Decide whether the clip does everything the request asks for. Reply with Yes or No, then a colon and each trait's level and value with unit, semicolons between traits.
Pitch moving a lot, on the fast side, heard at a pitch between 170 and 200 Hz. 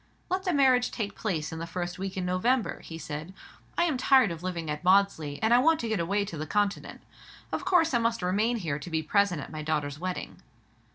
Yes: wide, 6.3 semitones; fast, 230 wpm; medium, 185 Hz